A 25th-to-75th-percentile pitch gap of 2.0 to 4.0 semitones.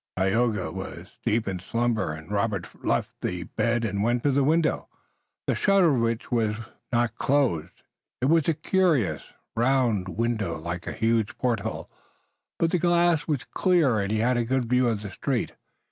No: average, 4.9 semitones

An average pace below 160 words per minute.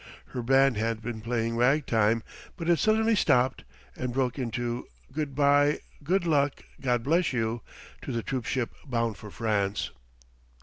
Yes: average, 150 wpm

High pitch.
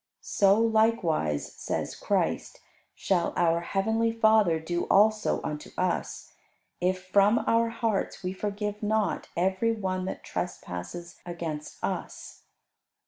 Yes: high, 195 Hz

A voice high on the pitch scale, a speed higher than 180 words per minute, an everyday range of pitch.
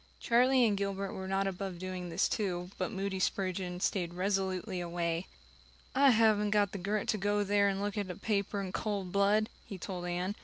No: high, 195 Hz; average, 195 wpm; narrow, 2.0 semitones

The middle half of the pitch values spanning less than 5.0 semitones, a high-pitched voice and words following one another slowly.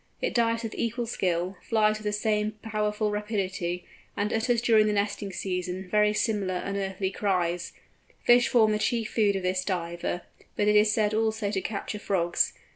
No: narrow, 2.5 semitones; high, 210 Hz; average, 175 wpm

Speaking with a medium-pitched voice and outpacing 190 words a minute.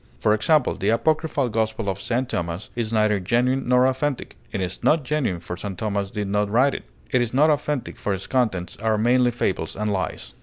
No: low, 110 Hz; fast, 205 wpm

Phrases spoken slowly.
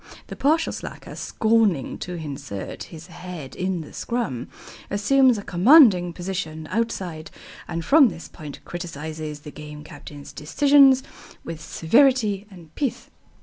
Yes: slow, 130 wpm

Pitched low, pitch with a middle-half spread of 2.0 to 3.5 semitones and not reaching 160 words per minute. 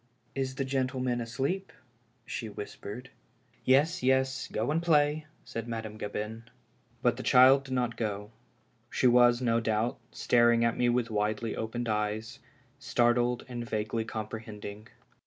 Yes: low, 120 Hz; average, 2.7 semitones; average, 145 wpm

